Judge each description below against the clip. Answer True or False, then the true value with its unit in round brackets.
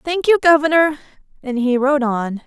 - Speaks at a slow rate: False (170 wpm)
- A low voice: False (285 Hz)